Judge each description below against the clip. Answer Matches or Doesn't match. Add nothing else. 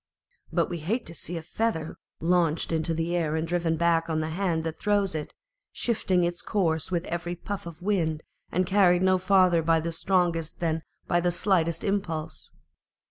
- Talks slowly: Doesn't match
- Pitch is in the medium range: Matches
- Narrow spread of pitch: Matches